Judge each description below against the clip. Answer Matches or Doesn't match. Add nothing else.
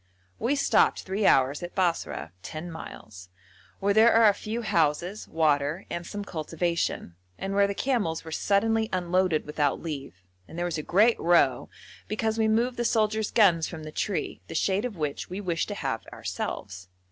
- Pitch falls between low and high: Matches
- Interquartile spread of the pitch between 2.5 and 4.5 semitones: Doesn't match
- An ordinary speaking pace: Matches